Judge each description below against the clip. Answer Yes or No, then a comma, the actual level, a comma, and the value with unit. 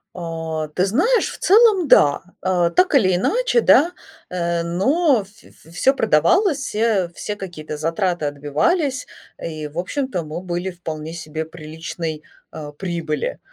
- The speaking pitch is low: No, medium, 175 Hz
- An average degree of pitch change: No, wide, 8.5 semitones